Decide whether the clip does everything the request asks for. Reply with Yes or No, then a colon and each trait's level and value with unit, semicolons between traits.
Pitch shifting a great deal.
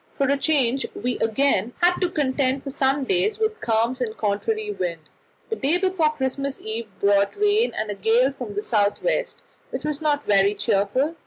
Yes: wide, 6.0 semitones